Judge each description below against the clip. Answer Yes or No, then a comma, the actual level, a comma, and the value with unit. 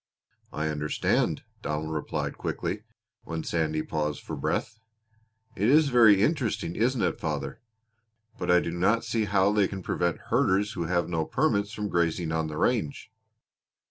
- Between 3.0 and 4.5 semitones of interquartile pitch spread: No, average, 5.1 semitones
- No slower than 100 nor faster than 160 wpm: Yes, average, 155 wpm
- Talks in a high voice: No, very low, 95 Hz